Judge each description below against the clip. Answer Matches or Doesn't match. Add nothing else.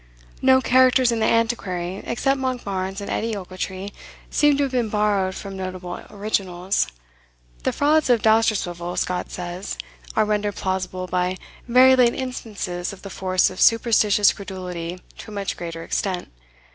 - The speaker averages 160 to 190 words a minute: Doesn't match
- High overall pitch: Matches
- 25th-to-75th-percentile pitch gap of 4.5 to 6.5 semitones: Doesn't match